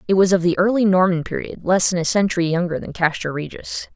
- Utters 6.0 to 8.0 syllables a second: Yes, 6.2 syllables/s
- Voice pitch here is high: No, medium, 180 Hz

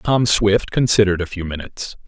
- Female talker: No, male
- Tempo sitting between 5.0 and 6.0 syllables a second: Yes, 5.6 syllables/s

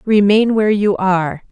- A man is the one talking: No, female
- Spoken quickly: No, average, 160 wpm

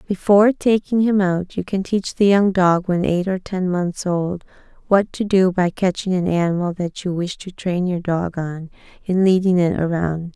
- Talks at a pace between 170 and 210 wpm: Yes, fast, 205 wpm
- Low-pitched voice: No, medium, 185 Hz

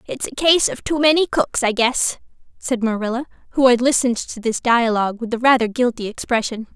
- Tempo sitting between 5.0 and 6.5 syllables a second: Yes, 5.7 syllables/s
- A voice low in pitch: No, high, 240 Hz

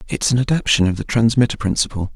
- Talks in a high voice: No, low, 115 Hz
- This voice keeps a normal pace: Yes, average, 195 wpm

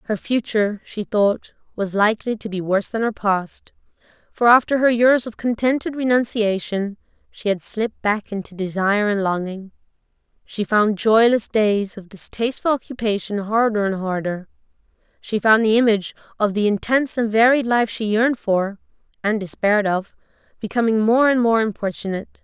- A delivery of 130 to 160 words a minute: Yes, average, 155 wpm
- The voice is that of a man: No, female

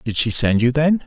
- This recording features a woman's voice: No, male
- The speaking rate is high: Yes, fast, 280 wpm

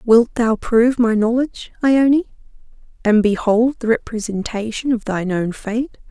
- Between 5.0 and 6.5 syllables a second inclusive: No, 4.6 syllables/s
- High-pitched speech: Yes, high, 230 Hz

